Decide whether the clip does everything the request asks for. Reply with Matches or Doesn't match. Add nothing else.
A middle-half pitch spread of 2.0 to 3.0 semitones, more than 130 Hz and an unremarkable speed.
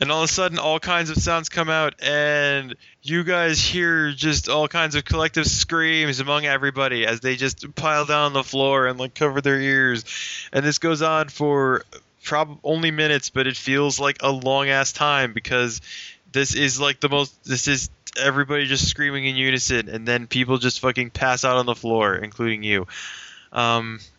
Matches